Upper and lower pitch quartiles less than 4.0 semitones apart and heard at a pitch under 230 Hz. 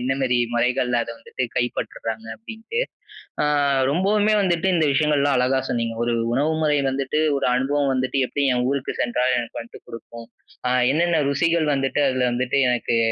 Yes: average, 3.6 semitones; low, 135 Hz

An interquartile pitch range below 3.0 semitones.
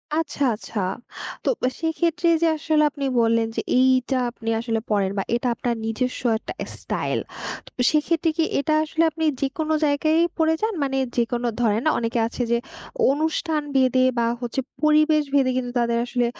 No: average, 4.8 semitones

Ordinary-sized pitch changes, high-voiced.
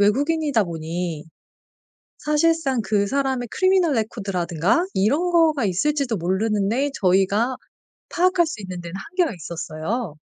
No: wide, 8.3 semitones; high, 225 Hz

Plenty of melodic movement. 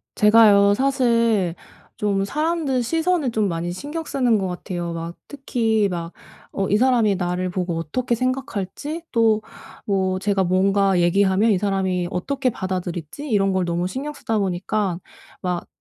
No: average, 5.0 semitones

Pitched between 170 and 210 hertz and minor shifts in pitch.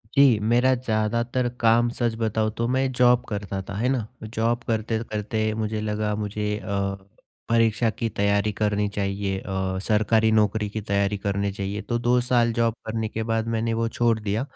No: low, 110 Hz; narrow, 2.1 semitones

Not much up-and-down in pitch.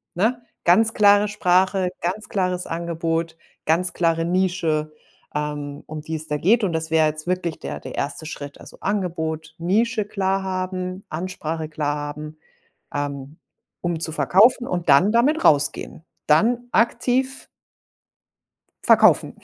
No: average, 4.1 semitones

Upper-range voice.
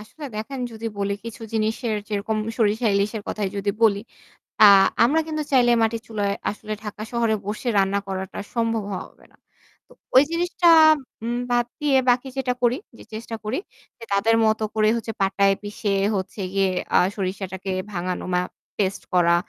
Yes: high, 215 Hz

